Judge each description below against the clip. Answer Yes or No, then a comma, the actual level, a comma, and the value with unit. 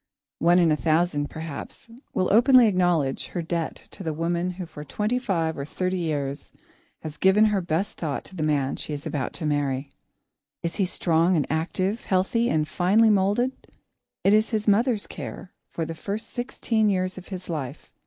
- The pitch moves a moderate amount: Yes, average, 4.5 semitones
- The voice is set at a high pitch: No, medium, 175 Hz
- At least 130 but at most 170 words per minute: No, average, 185 wpm